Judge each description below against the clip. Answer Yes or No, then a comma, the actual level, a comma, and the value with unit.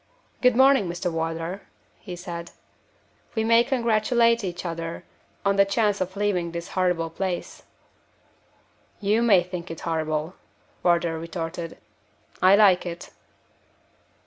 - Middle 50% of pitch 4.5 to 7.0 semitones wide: No, average, 3.5 semitones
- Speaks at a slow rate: Yes, slow, 120 wpm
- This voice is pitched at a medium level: Yes, medium, 180 Hz